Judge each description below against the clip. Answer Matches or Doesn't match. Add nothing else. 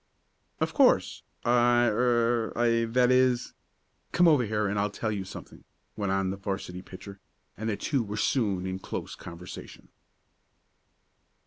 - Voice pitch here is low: Matches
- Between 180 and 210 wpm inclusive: Doesn't match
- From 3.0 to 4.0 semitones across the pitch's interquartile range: Matches